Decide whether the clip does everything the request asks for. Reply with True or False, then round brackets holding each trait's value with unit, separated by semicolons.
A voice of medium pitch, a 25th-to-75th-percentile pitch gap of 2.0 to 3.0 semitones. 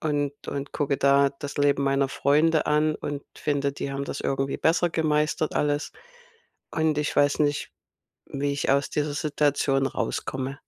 False (145 Hz; 1.4 semitones)